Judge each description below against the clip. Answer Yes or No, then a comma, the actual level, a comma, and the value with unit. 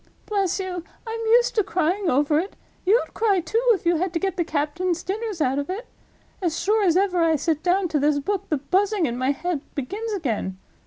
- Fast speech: Yes, fast, 215 wpm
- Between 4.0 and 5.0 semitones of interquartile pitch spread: Yes, average, 4.7 semitones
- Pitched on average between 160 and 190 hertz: No, very high, 360 Hz